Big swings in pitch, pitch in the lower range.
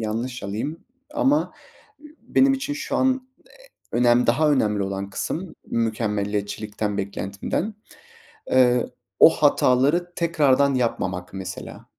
Yes: wide, 7.5 semitones; low, 120 Hz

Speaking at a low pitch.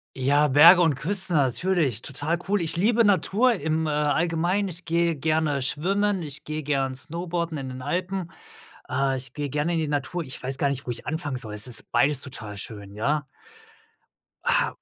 No: medium, 150 Hz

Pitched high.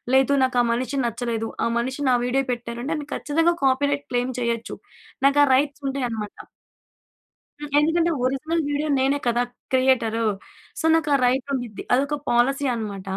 Yes: very high, 260 Hz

